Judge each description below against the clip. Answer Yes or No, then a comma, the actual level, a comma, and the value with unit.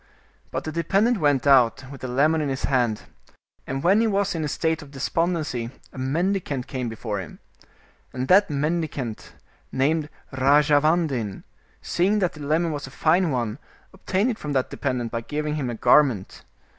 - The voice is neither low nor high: Yes, medium, 145 Hz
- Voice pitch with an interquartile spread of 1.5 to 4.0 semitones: No, average, 4.4 semitones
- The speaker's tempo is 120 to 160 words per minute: No, average, 170 wpm